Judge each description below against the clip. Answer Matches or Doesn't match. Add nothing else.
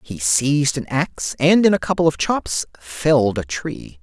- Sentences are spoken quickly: Doesn't match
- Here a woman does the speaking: Doesn't match